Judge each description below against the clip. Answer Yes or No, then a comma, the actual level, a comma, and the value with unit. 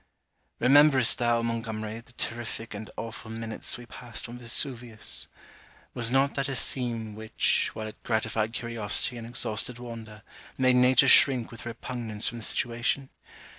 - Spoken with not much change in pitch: Yes, narrow, 1.8 semitones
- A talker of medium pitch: No, low, 115 Hz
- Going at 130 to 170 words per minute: Yes, average, 145 wpm